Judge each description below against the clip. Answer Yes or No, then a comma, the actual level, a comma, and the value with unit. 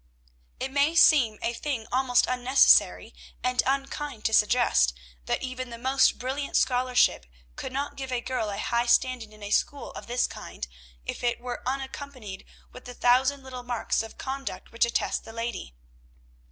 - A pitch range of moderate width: No, narrow, 2.3 semitones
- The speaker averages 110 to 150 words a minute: No, average, 165 wpm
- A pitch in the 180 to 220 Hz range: No, very high, 250 Hz